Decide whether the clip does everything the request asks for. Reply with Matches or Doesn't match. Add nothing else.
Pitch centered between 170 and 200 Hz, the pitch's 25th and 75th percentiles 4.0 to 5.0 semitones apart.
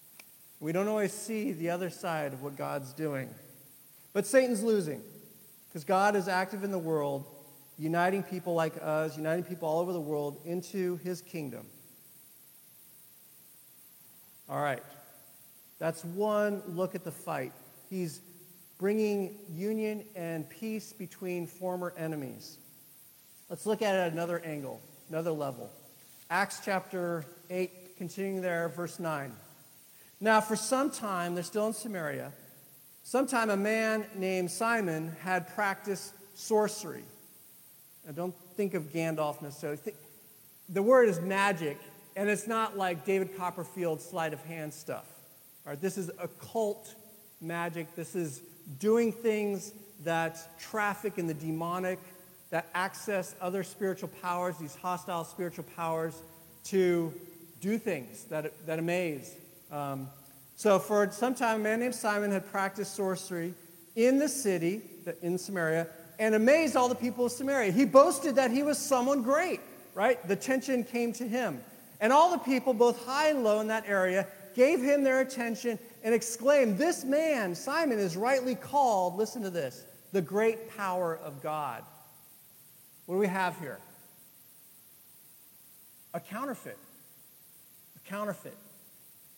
Matches